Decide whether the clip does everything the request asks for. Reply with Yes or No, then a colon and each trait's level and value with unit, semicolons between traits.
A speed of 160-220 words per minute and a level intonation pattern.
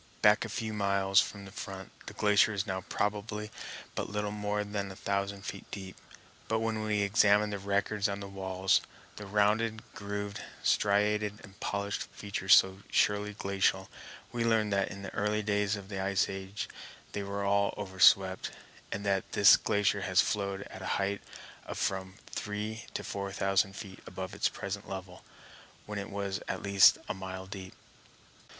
Yes: average, 175 wpm; narrow, 1.2 semitones